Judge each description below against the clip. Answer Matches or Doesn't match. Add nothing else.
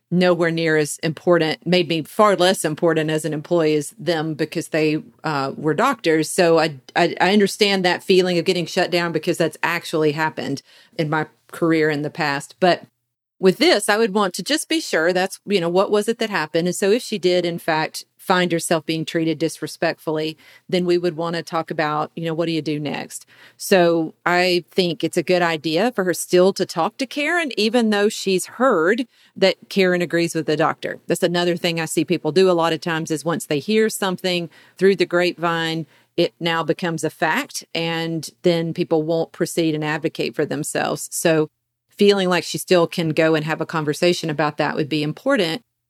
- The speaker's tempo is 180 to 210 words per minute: Matches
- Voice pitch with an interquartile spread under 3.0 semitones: Matches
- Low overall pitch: Doesn't match